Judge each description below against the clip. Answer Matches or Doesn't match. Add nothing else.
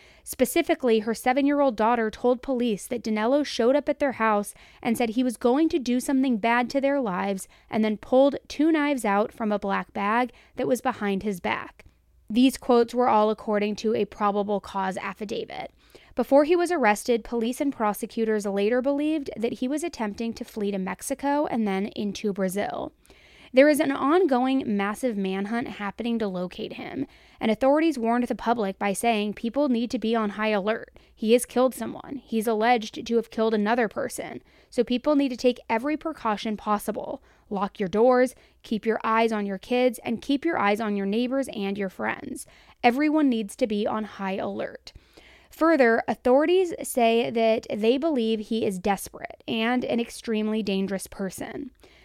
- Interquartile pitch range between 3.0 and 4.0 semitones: Matches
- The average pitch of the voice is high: Matches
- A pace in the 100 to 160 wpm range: Doesn't match